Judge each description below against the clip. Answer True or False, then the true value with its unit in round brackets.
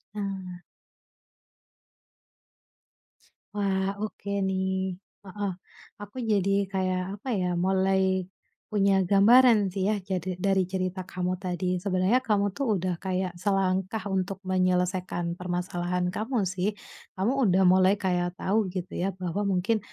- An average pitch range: False (1.5 semitones)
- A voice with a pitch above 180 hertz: True (190 Hz)